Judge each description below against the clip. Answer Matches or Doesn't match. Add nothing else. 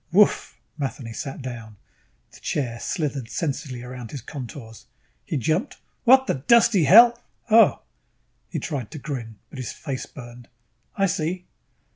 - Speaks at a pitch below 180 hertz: Matches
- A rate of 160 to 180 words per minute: Doesn't match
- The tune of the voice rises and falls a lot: Matches